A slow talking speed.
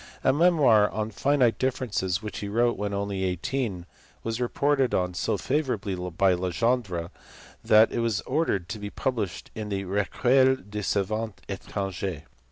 No: average, 155 wpm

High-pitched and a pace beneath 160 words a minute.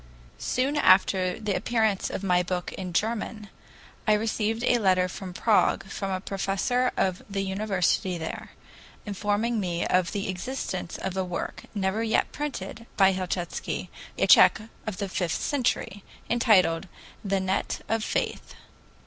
Yes: high, 195 Hz; average, 145 wpm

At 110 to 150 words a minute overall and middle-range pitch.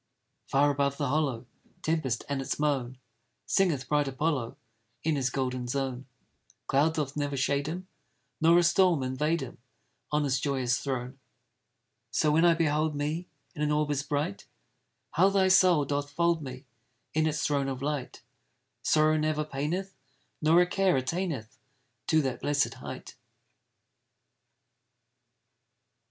Yes: average, 140 wpm; medium, 145 Hz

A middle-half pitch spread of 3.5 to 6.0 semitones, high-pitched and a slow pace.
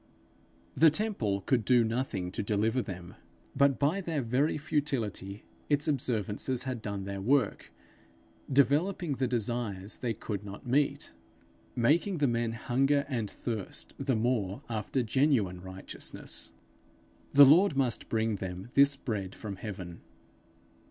No: wide, 5.5 semitones; low, 120 Hz; slow, 130 wpm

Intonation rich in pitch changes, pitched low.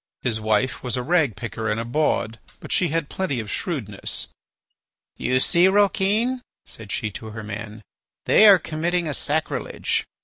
Yes: wide, 8.0 semitones; low, 130 Hz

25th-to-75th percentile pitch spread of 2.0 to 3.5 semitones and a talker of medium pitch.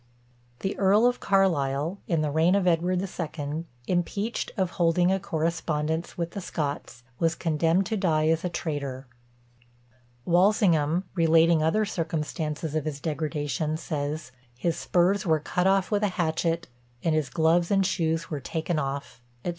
Yes: average, 2.9 semitones; medium, 165 Hz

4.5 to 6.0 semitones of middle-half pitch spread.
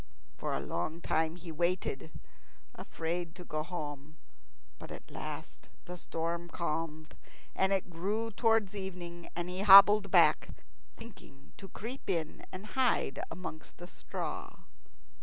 No: average, 3.2 semitones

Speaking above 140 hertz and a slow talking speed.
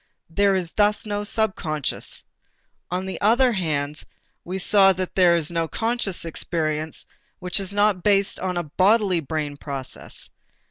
No: medium, 185 Hz; average, 145 wpm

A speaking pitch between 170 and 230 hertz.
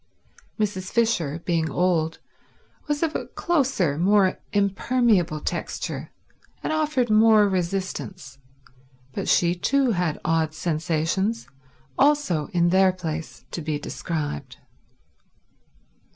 Yes: medium, 185 Hz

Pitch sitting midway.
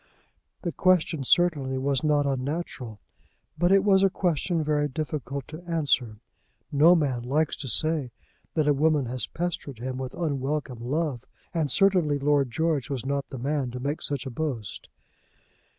Yes: medium, 145 Hz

